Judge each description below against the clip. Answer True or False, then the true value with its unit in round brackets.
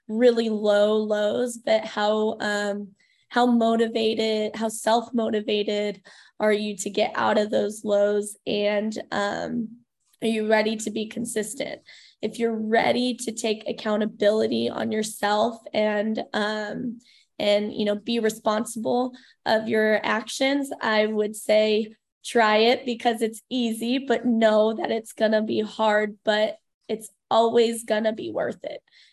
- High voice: True (220 Hz)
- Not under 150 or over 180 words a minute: False (140 wpm)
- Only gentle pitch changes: True (1.5 semitones)